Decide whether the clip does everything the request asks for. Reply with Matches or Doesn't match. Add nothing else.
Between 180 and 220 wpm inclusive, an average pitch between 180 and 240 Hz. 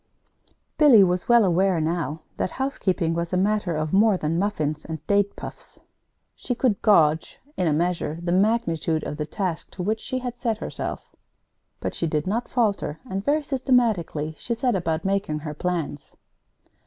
Doesn't match